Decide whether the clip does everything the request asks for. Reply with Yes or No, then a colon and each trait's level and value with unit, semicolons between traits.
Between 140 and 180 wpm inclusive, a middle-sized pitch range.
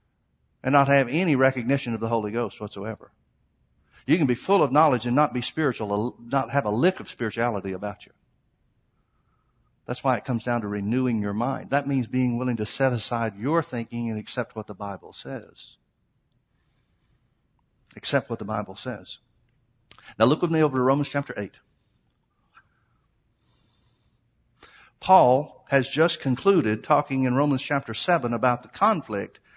Yes: average, 160 wpm; average, 4.0 semitones